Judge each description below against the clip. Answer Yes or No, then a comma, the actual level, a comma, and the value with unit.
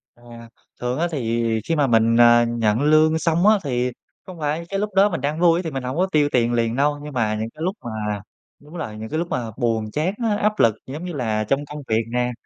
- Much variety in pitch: Yes, wide, 5.7 semitones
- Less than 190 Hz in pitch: Yes, low, 135 Hz